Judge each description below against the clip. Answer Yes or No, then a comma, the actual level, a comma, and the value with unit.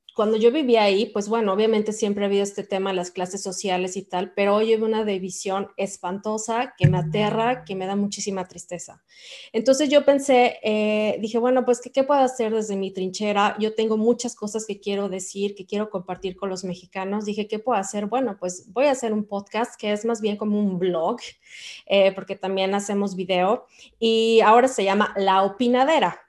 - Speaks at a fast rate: Yes, fast, 200 wpm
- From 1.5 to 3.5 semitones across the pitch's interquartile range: Yes, narrow, 2.6 semitones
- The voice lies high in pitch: Yes, high, 210 Hz